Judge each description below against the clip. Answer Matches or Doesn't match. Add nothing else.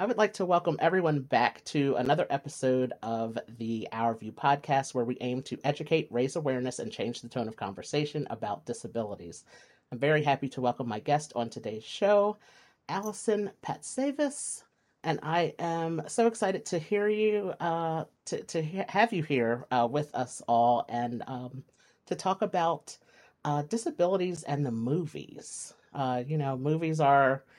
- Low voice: Doesn't match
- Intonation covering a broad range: Matches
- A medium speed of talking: Matches